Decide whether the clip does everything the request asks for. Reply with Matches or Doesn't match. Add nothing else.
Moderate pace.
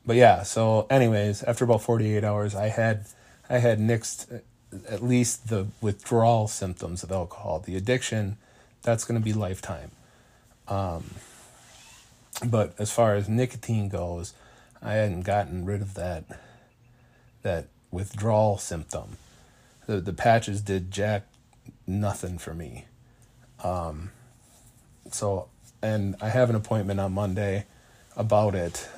Doesn't match